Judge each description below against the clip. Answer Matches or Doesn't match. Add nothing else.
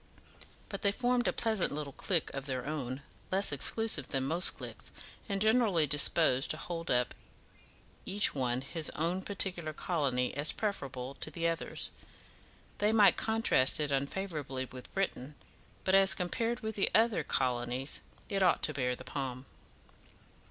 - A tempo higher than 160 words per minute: Doesn't match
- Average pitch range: Doesn't match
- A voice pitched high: Doesn't match